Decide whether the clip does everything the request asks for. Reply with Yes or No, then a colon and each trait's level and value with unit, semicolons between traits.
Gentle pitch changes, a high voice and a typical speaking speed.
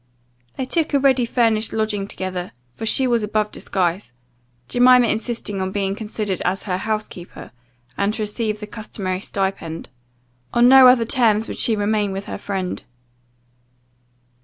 No: average, 3.2 semitones; high, 215 Hz; average, 155 wpm